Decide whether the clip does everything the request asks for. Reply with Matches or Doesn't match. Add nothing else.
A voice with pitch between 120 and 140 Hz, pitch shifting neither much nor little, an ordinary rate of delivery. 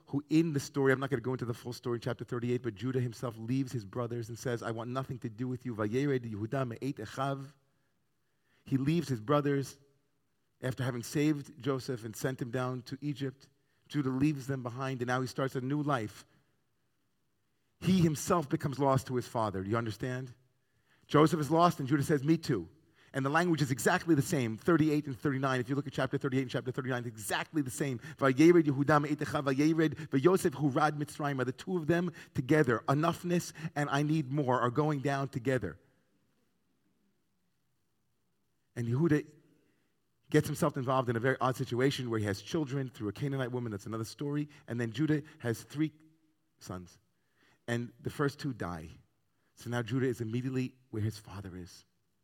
Matches